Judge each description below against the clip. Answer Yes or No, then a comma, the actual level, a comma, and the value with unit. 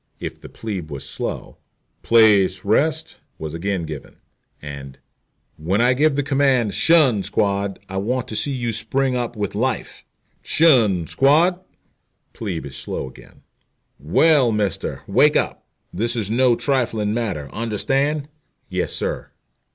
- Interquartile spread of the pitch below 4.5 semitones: No, wide, 5.4 semitones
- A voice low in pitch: Yes, low, 110 Hz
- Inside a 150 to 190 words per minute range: No, slow, 135 wpm